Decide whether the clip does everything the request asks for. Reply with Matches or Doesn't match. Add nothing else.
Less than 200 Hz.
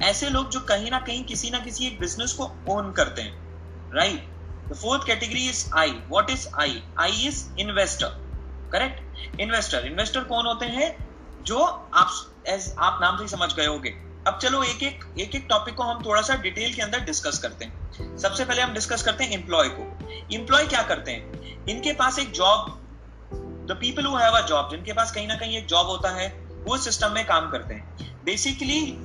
Doesn't match